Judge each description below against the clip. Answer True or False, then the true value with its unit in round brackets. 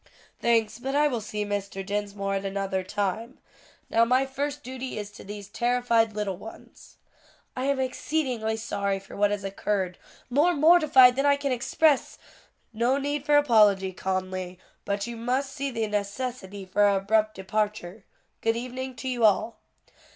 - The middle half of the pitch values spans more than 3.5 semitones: True (4.5 semitones)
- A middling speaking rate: True (165 wpm)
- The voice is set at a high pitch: True (225 Hz)